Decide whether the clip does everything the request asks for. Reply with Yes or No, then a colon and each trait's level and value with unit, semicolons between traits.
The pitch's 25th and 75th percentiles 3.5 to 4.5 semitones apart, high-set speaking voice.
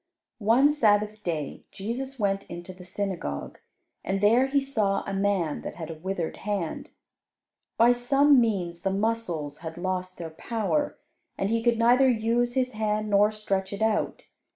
Yes: average, 4.0 semitones; high, 205 Hz